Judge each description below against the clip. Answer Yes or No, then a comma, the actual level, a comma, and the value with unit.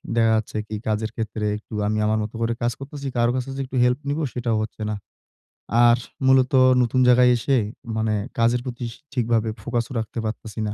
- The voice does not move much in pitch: Yes, narrow, 2.2 semitones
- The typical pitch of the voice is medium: No, low, 120 Hz